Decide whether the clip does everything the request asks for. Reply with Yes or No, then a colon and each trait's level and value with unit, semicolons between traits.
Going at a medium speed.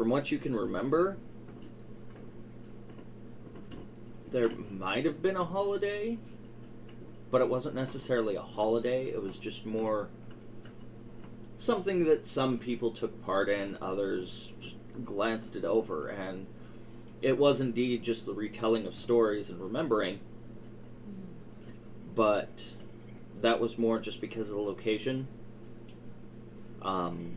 No: slow, 120 wpm